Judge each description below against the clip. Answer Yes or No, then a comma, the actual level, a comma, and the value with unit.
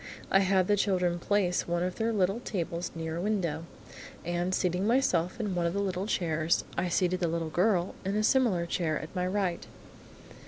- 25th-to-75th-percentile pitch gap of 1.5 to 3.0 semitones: Yes, narrow, 2.6 semitones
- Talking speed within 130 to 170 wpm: No, average, 195 wpm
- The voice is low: No, medium, 180 Hz